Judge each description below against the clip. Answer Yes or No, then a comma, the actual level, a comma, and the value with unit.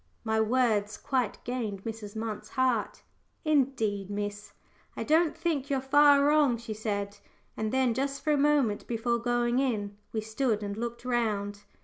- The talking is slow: No, average, 155 wpm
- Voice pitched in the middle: No, high, 235 Hz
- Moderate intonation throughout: Yes, average, 4.1 semitones